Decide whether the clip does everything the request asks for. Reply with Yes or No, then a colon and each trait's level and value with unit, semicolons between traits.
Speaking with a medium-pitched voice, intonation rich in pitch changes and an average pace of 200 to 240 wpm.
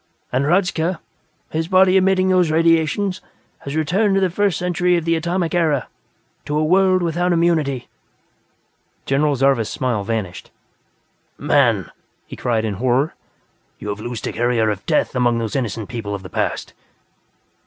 No: medium, 155 Hz; wide, 6.7 semitones; average, 155 wpm